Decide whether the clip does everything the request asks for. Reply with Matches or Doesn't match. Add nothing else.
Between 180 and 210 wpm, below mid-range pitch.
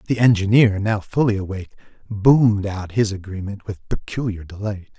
Doesn't match